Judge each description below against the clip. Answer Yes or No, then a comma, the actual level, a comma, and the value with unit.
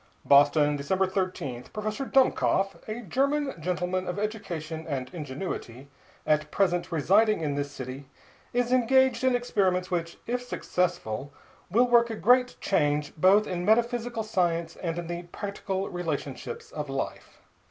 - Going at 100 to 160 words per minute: Yes, average, 140 wpm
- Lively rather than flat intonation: Yes, wide, 6.6 semitones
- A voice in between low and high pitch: Yes, medium, 180 Hz